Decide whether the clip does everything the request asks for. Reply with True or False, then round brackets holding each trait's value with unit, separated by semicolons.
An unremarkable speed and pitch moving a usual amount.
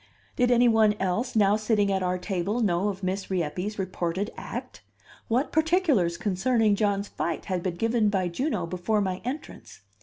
True (170 wpm; 3.6 semitones)